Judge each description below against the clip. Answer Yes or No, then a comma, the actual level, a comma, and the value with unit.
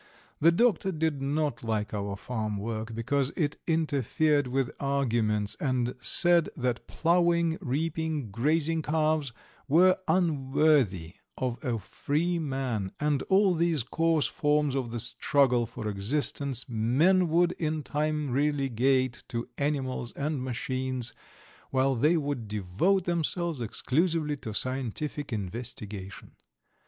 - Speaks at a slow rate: Yes, slow, 120 wpm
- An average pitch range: Yes, average, 4.9 semitones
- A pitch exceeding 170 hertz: No, medium, 140 Hz